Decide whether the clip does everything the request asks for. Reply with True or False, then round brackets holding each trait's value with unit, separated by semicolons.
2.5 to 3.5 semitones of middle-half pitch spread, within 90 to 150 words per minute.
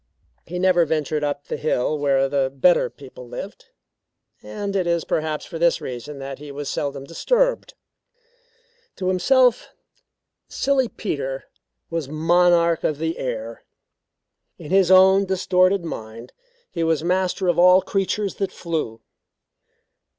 False (4.8 semitones; 135 wpm)